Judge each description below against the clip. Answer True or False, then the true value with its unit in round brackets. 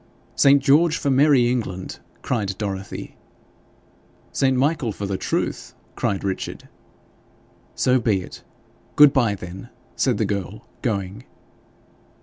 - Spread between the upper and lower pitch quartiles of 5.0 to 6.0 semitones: True (5.5 semitones)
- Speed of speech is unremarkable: False (120 wpm)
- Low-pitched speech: True (115 Hz)